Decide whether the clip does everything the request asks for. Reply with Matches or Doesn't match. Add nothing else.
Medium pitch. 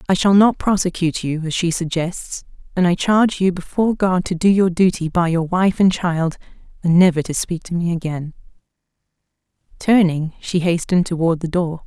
Matches